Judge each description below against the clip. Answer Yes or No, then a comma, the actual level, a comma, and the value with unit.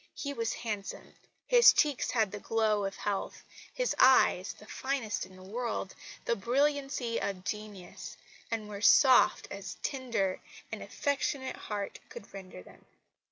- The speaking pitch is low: No, high, 220 Hz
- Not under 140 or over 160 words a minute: Yes, average, 150 wpm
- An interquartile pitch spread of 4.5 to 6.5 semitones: Yes, average, 4.8 semitones